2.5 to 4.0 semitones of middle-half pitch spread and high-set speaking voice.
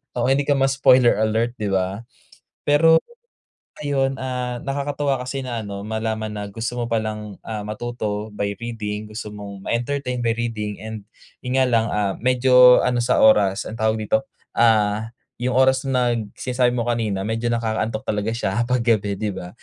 No: average, 2.9 semitones; low, 115 Hz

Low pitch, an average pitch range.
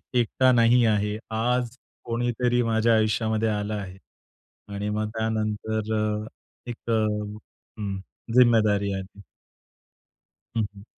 No: low, 110 Hz; narrow, 1.7 semitones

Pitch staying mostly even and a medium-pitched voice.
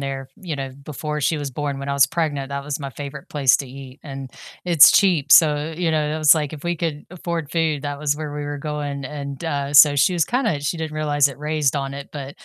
Yes: narrow, 1.9 semitones; medium, 145 Hz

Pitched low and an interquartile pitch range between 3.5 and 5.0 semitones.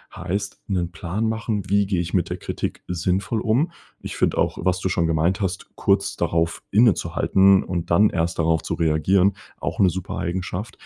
No: very low, 95 Hz; average, 2.7 semitones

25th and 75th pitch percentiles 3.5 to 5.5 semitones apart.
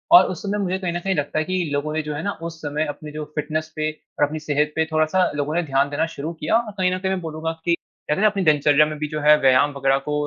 No: average, 2.9 semitones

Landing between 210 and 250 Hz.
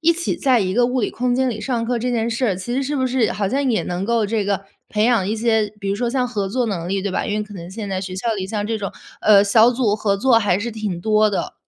Yes: high, 220 Hz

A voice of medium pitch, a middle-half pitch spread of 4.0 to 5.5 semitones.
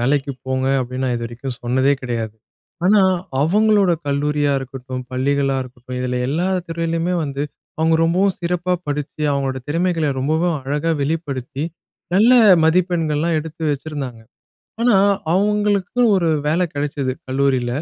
Yes: medium, 145 Hz; average, 4.5 semitones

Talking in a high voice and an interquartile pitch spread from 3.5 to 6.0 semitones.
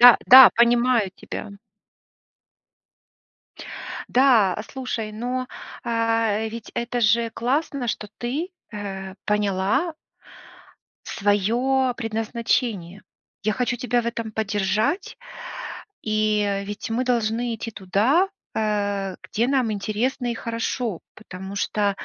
No: high, 225 Hz; average, 2.9 semitones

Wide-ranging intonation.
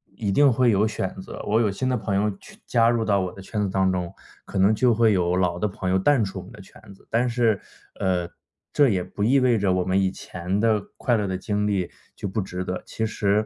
No: average, 3.3 semitones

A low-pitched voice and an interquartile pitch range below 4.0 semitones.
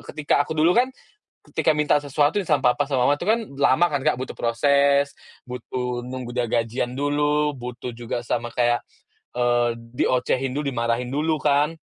Yes: low, 130 Hz; average, 3.2 semitones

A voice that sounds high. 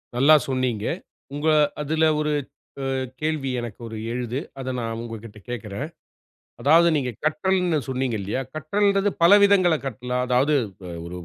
No: low, 135 Hz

